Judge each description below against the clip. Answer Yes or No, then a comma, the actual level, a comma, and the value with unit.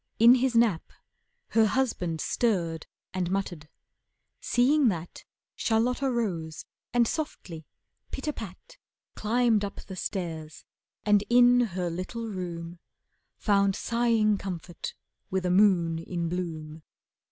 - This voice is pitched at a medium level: No, high, 195 Hz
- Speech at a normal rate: No, slow, 120 wpm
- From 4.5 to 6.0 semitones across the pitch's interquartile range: Yes, wide, 5.5 semitones